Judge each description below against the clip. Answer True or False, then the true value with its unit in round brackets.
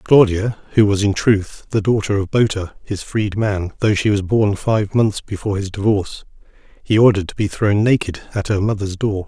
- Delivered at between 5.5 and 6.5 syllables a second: False (5.1 syllables/s)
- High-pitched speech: False (100 Hz)